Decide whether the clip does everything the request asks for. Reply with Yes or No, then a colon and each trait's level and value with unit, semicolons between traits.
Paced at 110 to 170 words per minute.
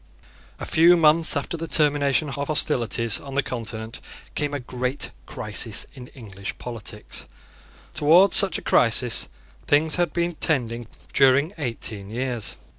Yes: slow, 135 wpm